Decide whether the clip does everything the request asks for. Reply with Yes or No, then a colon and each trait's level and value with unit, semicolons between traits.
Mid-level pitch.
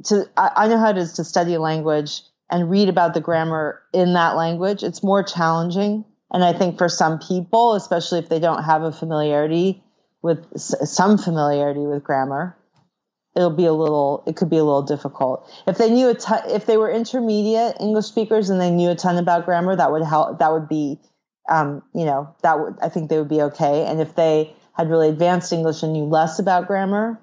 Yes: medium, 170 Hz